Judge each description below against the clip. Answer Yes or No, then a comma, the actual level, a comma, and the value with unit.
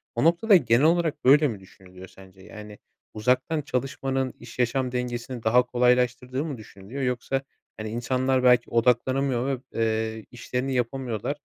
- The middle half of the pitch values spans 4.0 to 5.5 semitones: No, narrow, 2.6 semitones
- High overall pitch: No, low, 125 Hz